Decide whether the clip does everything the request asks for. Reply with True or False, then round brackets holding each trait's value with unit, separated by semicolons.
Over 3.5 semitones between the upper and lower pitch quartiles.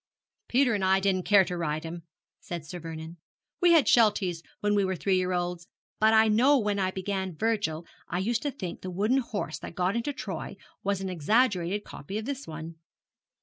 True (3.9 semitones)